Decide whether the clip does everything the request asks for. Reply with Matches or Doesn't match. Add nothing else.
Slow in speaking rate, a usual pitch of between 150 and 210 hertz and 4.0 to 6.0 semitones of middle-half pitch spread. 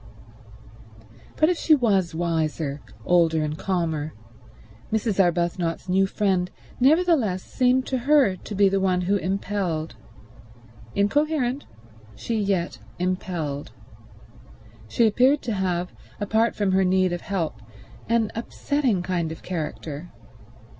Matches